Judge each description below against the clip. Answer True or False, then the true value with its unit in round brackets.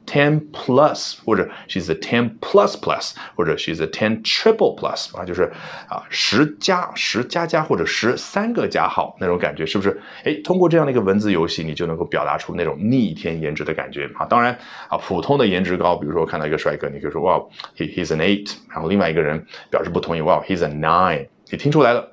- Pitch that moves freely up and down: True (8.9 semitones)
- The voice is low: True (100 Hz)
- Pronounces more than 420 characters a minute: True (430 characters per minute)